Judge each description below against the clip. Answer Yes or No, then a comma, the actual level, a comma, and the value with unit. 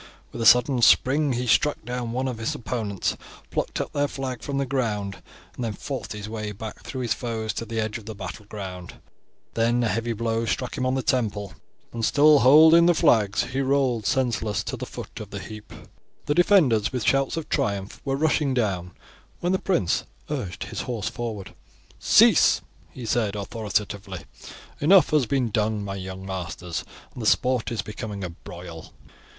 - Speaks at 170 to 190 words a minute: Yes, average, 185 wpm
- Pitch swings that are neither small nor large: Yes, average, 4.1 semitones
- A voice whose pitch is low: Yes, low, 115 Hz